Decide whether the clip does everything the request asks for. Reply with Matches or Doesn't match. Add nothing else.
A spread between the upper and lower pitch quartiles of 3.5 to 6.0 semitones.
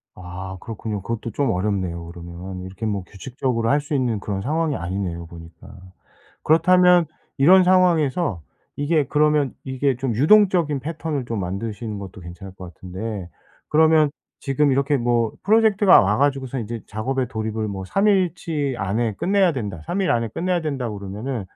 Doesn't match